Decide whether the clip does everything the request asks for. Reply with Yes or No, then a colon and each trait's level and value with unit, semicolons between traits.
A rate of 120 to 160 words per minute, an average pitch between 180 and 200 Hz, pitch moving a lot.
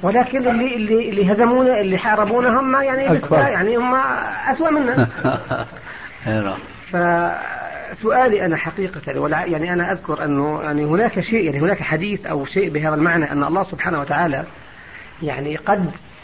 Yes: average, 130 wpm; high, 190 Hz; wide, 7.3 semitones